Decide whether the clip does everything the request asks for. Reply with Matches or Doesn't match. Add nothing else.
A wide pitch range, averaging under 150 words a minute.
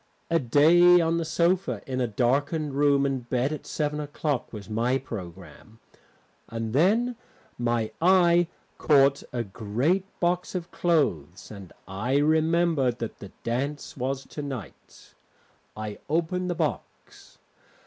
Matches